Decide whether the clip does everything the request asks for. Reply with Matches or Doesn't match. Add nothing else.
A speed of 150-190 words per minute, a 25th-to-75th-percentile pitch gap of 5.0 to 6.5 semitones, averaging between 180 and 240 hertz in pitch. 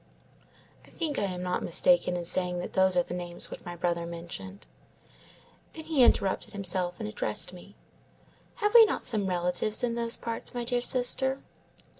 Matches